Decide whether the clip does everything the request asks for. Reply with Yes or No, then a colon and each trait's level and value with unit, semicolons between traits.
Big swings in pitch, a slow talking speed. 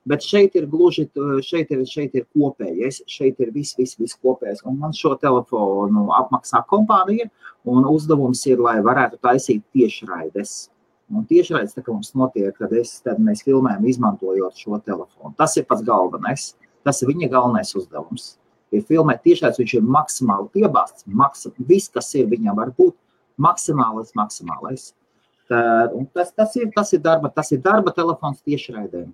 No: wide, 6.2 semitones; average, 145 wpm